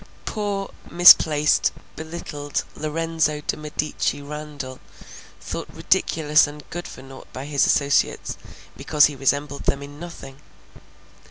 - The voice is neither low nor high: Yes, medium, 150 Hz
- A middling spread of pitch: No, narrow, 2.0 semitones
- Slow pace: Yes, slow, 115 wpm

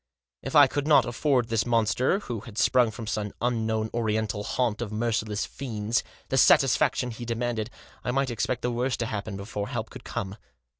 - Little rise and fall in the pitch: Yes, narrow, 2.3 semitones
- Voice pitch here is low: Yes, low, 115 Hz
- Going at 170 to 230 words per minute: Yes, average, 190 wpm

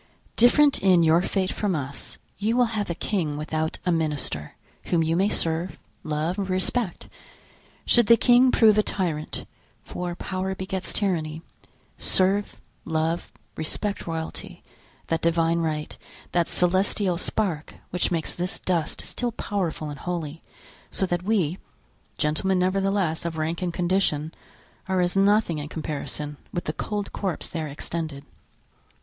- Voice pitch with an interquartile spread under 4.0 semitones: Yes, average, 3.5 semitones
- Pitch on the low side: No, medium, 175 Hz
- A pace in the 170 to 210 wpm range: No, slow, 135 wpm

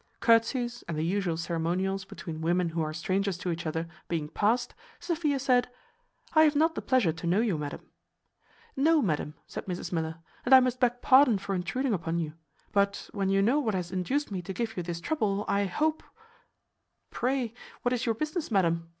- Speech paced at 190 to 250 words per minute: Yes, average, 195 wpm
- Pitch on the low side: No, high, 200 Hz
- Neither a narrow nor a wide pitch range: No, wide, 6.8 semitones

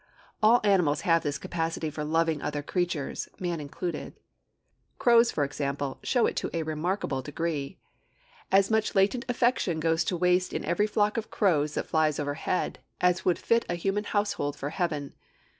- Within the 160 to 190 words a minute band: Yes, average, 165 wpm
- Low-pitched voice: No, medium, 170 Hz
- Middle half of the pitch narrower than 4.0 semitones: No, average, 4.7 semitones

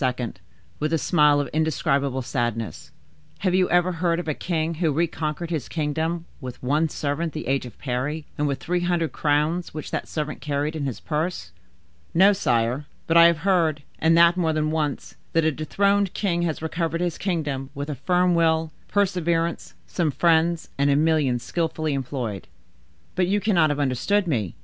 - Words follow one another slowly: No, average, 175 wpm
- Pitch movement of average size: Yes, average, 3.1 semitones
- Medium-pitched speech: Yes, medium, 160 Hz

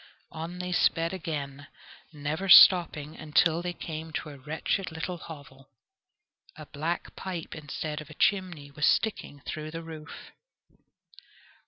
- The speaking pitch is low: No, medium, 160 Hz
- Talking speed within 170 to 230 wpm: No, slow, 135 wpm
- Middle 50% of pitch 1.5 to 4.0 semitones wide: Yes, narrow, 2.5 semitones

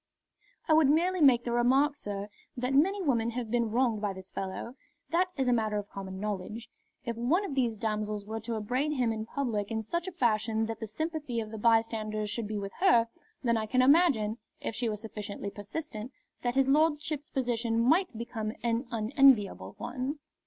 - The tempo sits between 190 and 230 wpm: Yes, average, 195 wpm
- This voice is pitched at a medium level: No, high, 235 Hz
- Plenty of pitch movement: No, average, 4.1 semitones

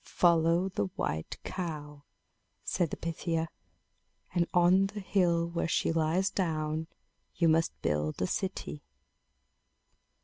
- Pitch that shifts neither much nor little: No, narrow, 2.3 semitones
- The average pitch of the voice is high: No, medium, 165 Hz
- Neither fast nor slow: No, slow, 115 wpm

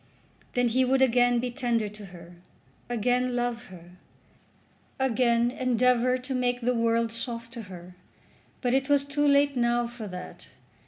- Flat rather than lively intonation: Yes, narrow, 1.7 semitones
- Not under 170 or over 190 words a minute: No, average, 155 wpm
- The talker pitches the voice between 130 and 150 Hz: No, high, 240 Hz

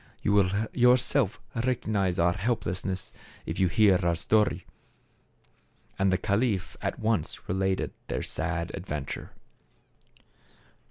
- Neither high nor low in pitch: No, very low, 95 Hz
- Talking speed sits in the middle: No, slow, 110 wpm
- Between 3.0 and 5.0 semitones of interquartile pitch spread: Yes, average, 3.4 semitones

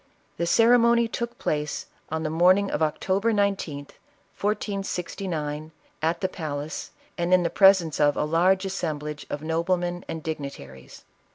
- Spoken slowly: Yes, slow, 130 wpm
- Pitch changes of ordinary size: Yes, average, 4.2 semitones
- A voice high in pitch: No, medium, 170 Hz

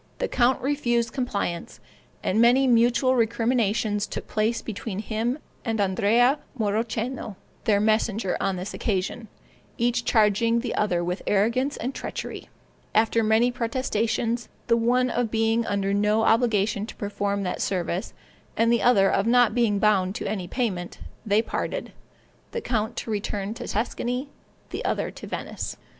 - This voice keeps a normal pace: Yes, average, 150 wpm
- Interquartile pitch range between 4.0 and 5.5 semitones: No, average, 2.8 semitones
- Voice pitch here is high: Yes, high, 225 Hz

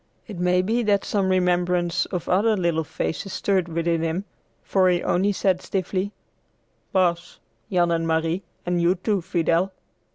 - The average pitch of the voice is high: No, medium, 180 Hz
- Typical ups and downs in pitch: No, narrow, 2.0 semitones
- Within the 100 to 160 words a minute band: Yes, average, 155 wpm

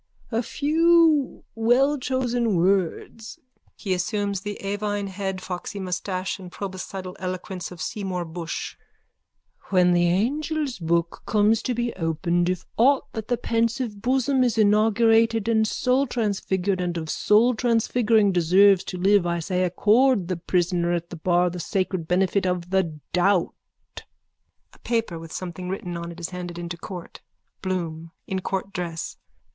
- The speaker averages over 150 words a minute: No, average, 140 wpm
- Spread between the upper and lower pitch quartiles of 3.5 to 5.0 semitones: Yes, average, 4.2 semitones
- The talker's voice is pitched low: No, high, 190 Hz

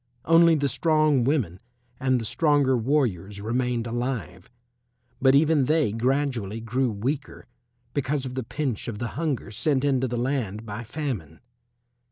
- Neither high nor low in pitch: No, low, 130 Hz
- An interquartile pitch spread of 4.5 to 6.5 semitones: No, average, 4.1 semitones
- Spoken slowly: No, average, 145 wpm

